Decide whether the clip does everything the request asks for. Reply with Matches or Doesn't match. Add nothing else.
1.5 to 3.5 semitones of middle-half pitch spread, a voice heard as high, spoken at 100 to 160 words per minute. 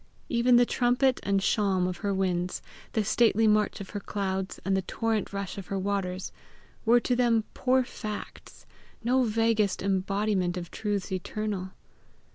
Matches